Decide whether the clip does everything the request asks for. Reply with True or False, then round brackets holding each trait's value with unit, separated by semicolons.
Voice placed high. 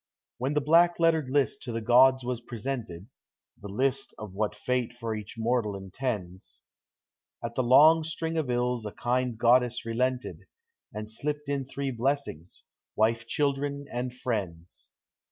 False (125 Hz)